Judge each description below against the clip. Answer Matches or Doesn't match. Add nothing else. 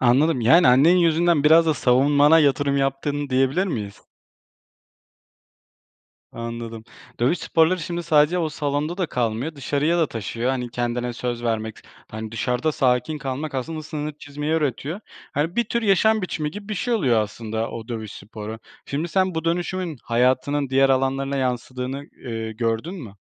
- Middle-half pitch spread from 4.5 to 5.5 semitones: Matches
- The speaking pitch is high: Doesn't match